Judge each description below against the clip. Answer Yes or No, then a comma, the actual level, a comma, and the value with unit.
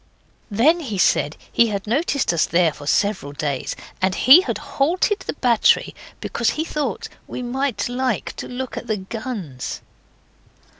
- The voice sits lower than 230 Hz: No, high, 235 Hz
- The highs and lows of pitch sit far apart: Yes, wide, 6.7 semitones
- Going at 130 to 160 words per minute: Yes, average, 155 wpm